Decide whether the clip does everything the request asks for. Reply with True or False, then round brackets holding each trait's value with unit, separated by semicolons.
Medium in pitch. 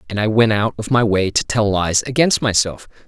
False (110 Hz)